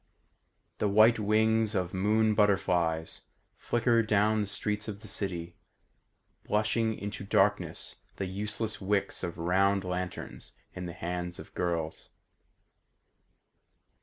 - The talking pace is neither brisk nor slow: No, slow, 115 wpm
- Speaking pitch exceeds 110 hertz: No, low, 100 Hz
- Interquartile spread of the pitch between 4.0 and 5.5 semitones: No, average, 3.1 semitones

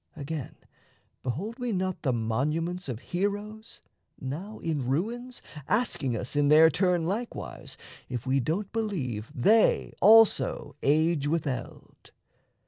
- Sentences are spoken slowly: Yes, slow, 125 wpm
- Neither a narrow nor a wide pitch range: No, wide, 7.3 semitones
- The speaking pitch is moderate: Yes, medium, 165 Hz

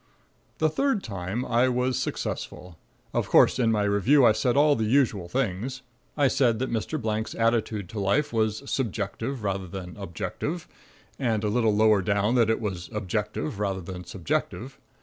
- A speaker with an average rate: Yes, average, 170 wpm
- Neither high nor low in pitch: No, low, 110 Hz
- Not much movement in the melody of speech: No, average, 4.1 semitones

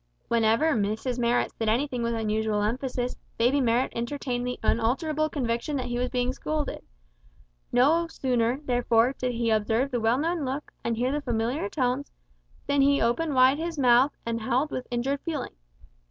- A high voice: Yes, very high, 250 Hz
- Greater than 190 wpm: No, average, 170 wpm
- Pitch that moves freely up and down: No, average, 3.3 semitones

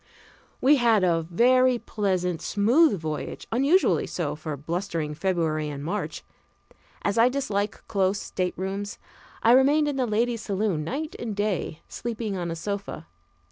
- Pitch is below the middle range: No, high, 200 Hz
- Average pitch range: No, wide, 5.8 semitones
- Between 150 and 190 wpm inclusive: No, average, 140 wpm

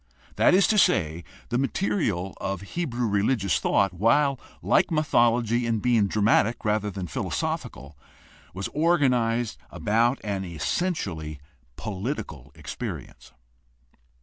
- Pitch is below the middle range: Yes, low, 115 Hz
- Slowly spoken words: Yes, slow, 110 wpm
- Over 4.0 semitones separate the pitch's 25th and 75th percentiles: Yes, average, 4.9 semitones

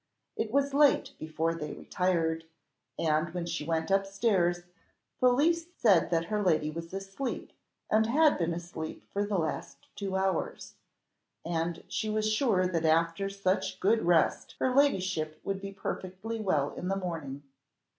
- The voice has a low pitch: No, medium, 185 Hz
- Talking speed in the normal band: Yes, average, 155 wpm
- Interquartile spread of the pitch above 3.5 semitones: Yes, average, 4.3 semitones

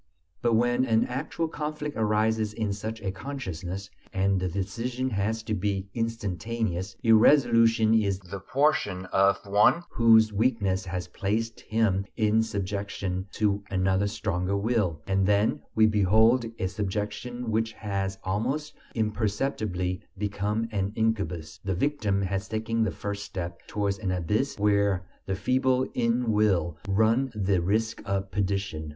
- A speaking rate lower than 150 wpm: Yes, average, 140 wpm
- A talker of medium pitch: No, low, 105 Hz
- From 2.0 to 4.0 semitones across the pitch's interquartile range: Yes, average, 2.7 semitones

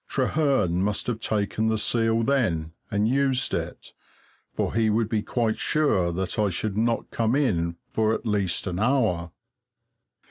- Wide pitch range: No, average, 3.8 semitones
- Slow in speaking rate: No, average, 155 wpm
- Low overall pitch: Yes, low, 110 Hz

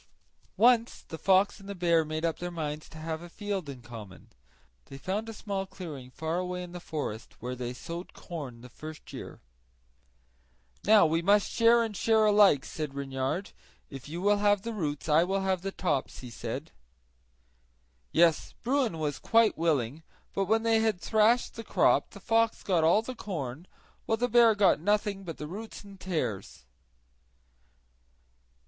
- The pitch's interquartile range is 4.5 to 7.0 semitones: Yes, wide, 5.4 semitones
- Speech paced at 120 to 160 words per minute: No, average, 175 wpm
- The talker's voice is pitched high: No, medium, 180 Hz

